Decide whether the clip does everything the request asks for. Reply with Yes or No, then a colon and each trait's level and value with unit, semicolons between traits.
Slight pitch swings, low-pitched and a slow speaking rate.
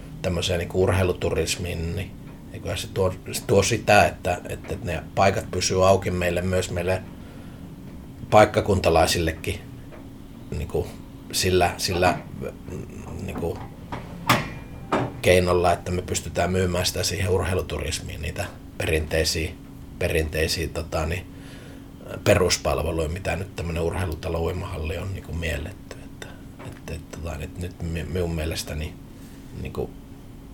No: narrow, 1.9 semitones; very low, 90 Hz; average, 105 wpm